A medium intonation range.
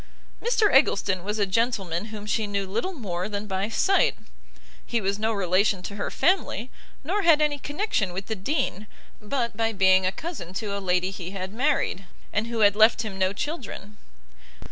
Yes: average, 4.0 semitones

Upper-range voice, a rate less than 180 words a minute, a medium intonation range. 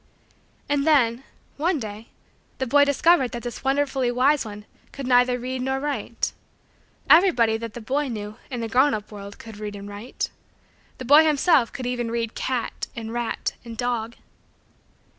Yes: high, 245 Hz; average, 165 wpm; average, 3.5 semitones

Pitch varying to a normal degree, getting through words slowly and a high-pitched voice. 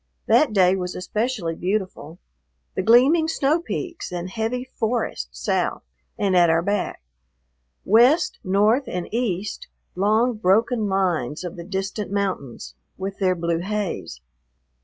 Yes: average, 4.3 semitones; slow, 130 wpm; high, 195 Hz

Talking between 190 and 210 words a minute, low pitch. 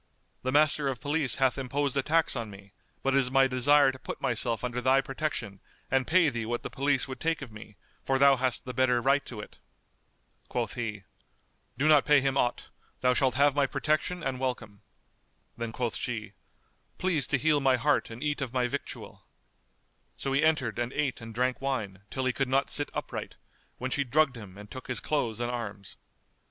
Yes: fast, 205 wpm; low, 130 Hz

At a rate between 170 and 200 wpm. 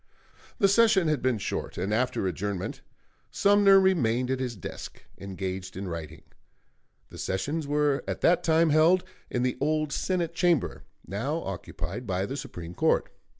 No: average, 150 wpm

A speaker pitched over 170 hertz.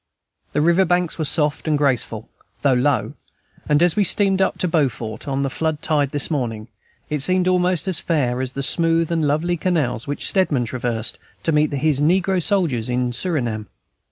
No: medium, 150 Hz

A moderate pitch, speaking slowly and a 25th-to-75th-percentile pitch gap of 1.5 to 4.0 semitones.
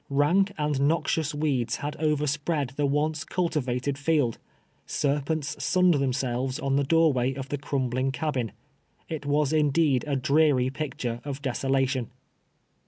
No: medium, 145 Hz; average, 145 wpm; narrow, 2.5 semitones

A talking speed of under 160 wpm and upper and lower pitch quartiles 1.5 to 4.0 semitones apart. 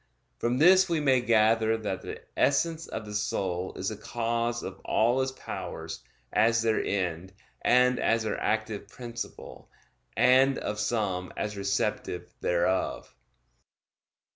Yes: slow, 135 wpm; average, 3.4 semitones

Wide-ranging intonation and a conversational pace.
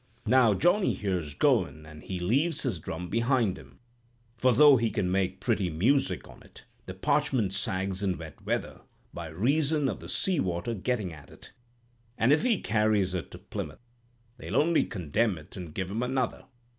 Yes: wide, 6.2 semitones; average, 180 wpm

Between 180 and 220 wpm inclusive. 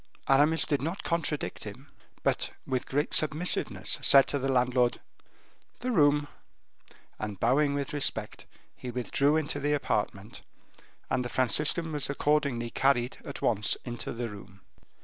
No: average, 140 wpm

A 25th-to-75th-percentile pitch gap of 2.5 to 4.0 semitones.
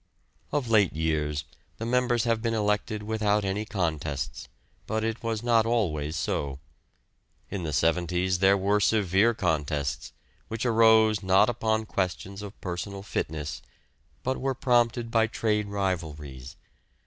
No: average, 5.2 semitones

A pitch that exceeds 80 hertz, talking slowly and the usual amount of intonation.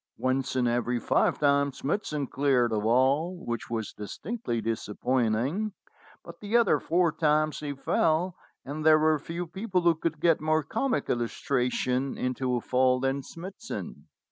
No: medium, 140 Hz; average, 150 wpm; average, 4.8 semitones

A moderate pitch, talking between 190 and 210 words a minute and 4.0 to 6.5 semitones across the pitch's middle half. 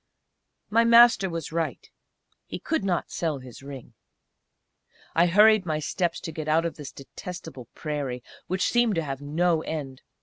No: medium, 165 Hz; average, 160 wpm; average, 4.5 semitones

